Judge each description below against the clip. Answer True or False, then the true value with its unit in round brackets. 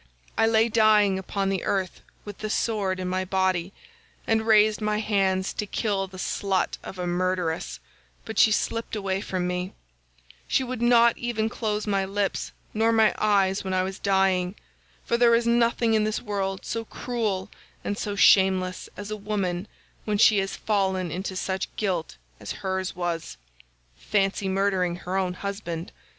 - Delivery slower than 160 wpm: False (165 wpm)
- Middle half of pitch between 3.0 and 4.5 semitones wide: False (2.4 semitones)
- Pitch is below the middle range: False (195 Hz)